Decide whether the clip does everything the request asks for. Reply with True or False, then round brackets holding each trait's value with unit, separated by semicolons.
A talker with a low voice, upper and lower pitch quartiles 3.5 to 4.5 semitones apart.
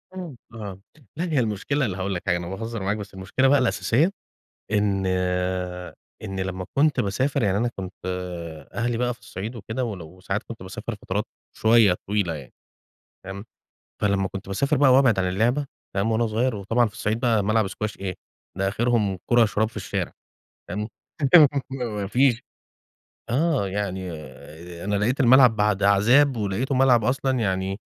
True (110 Hz; 4.0 semitones)